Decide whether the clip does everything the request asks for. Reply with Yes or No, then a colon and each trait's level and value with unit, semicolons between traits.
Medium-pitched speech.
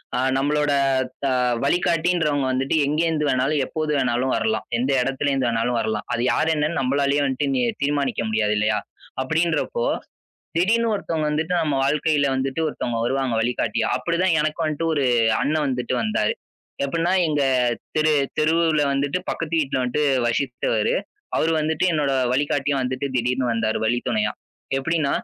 Yes: medium, 145 Hz